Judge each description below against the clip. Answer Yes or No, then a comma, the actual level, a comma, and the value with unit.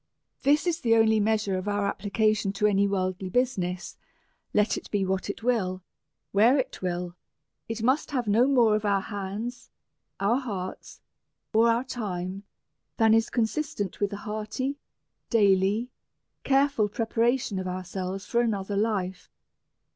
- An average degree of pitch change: Yes, average, 3.3 semitones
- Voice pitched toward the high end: Yes, high, 210 Hz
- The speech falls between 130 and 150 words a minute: Yes, average, 145 wpm